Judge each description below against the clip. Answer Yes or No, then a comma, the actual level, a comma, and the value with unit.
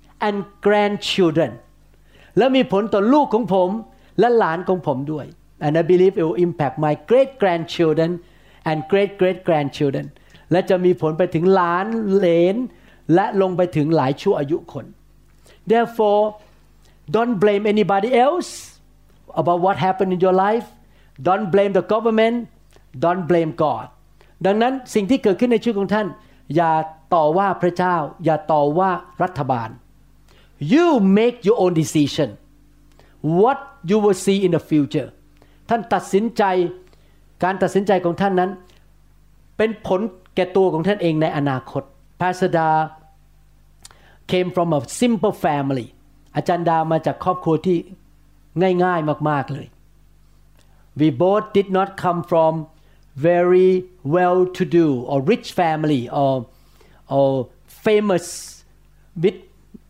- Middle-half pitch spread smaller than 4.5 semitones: No, average, 4.8 semitones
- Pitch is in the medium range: Yes, medium, 175 Hz